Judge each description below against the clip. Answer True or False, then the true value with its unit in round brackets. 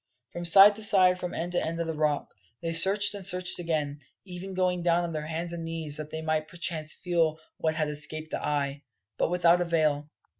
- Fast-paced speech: True (215 wpm)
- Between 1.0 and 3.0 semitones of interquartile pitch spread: True (2.4 semitones)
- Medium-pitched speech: True (165 Hz)